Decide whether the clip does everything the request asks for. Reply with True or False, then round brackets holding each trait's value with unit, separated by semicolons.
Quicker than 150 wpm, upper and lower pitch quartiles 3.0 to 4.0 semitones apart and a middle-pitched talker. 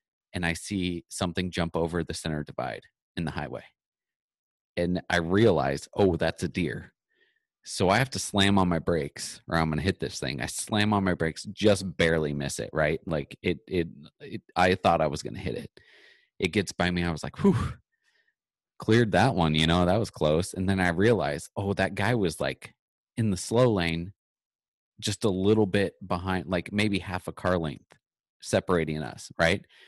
False (195 wpm; 3.3 semitones; 90 Hz)